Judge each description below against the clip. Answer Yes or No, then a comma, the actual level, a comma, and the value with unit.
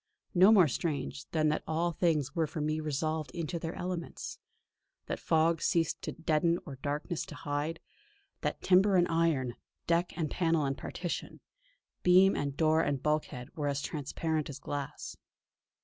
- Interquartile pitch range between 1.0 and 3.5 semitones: Yes, narrow, 2.5 semitones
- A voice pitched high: No, medium, 160 Hz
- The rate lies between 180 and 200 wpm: No, average, 160 wpm